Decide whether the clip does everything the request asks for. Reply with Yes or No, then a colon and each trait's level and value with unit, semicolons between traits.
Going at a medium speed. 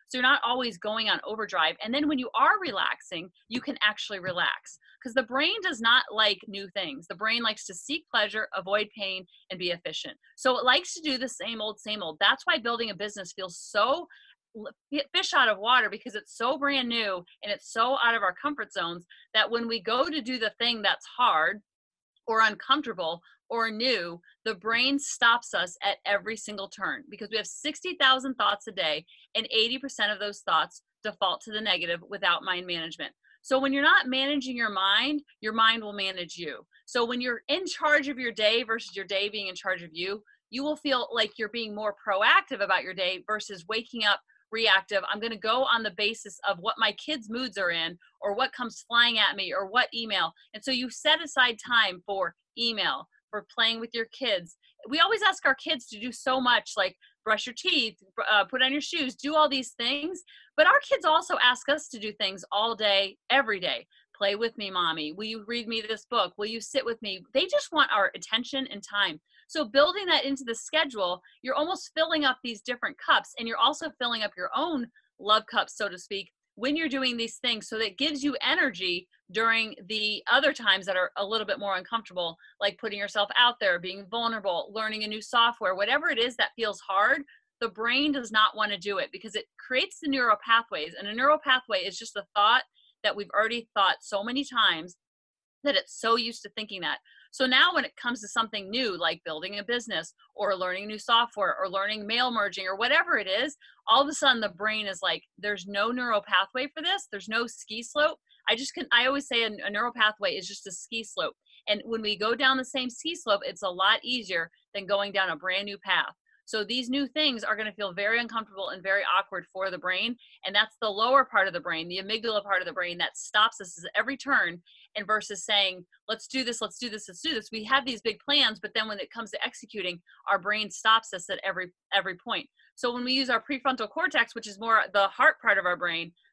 No: fast, 225 wpm